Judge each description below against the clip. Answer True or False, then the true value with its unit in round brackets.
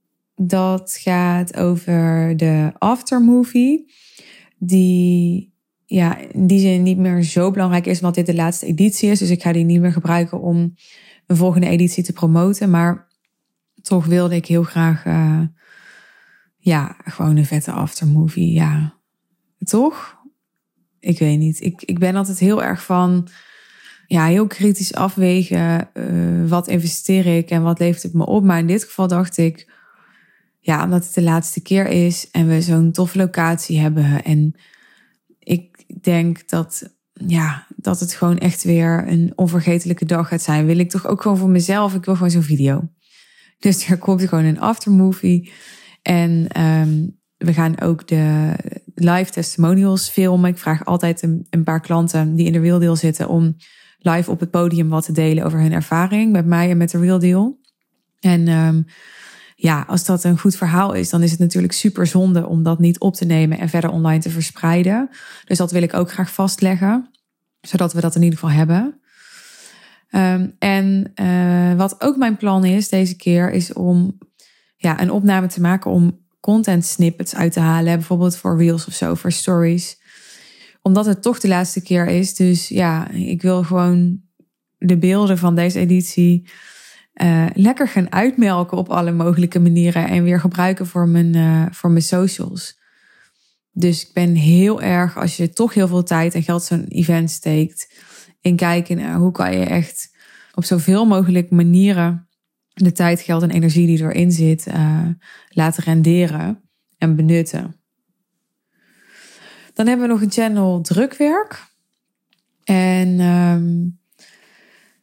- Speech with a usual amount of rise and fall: False (2.1 semitones)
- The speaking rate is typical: True (165 wpm)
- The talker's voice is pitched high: False (175 Hz)